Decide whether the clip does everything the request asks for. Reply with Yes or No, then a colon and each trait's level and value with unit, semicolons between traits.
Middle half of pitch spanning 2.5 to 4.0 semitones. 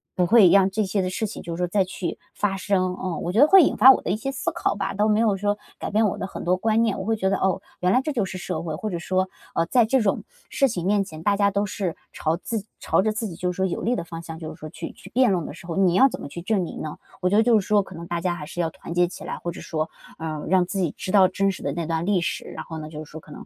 Yes: average, 3.3 semitones